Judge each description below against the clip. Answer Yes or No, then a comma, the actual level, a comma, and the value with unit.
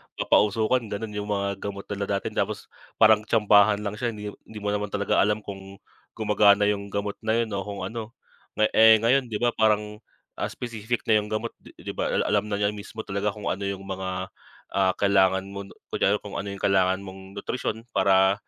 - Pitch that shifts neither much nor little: No, narrow, 1.6 semitones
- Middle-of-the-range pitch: No, low, 105 Hz